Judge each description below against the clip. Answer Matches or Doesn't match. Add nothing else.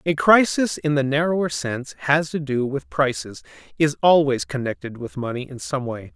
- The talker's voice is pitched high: Doesn't match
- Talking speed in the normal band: Matches